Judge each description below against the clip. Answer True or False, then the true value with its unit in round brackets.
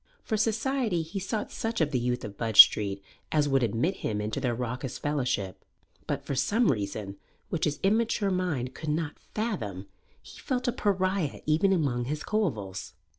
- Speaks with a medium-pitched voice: True (150 Hz)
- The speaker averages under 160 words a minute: False (175 wpm)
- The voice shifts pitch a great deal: True (8.6 semitones)